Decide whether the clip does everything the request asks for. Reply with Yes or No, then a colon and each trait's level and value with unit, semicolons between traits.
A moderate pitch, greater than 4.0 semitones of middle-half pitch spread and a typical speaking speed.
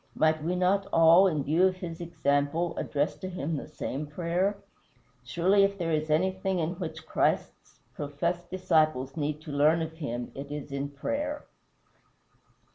No: medium, 160 Hz; average, 3.7 semitones; average, 160 wpm